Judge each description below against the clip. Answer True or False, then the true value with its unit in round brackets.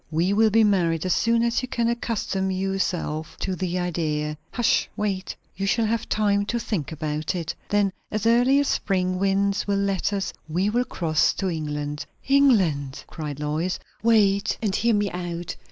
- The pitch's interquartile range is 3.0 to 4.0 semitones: False (4.5 semitones)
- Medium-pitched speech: False (195 Hz)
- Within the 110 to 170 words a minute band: False (180 wpm)